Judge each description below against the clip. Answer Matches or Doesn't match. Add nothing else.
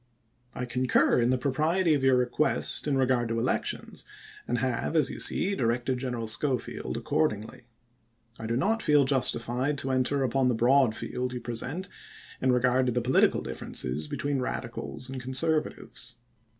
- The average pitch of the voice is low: Matches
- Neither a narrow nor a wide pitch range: Doesn't match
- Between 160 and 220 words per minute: Matches